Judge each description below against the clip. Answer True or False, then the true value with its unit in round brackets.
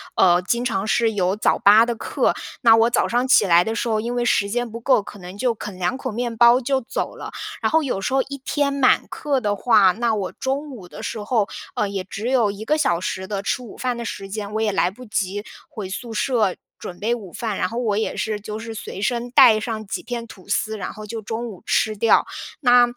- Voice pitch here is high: True (220 Hz)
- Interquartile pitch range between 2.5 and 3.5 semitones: True (3.1 semitones)